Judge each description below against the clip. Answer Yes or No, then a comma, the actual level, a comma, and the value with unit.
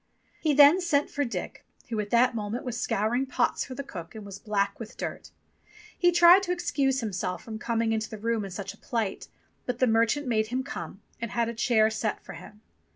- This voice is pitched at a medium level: No, high, 230 Hz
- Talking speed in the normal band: No, fast, 220 wpm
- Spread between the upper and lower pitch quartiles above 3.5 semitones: Yes, average, 3.9 semitones